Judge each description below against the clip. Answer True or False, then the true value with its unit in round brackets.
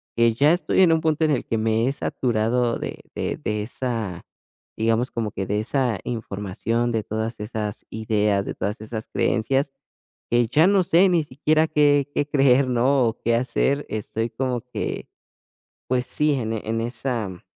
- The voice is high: False (120 Hz)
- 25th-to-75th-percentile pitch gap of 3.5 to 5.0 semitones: True (3.9 semitones)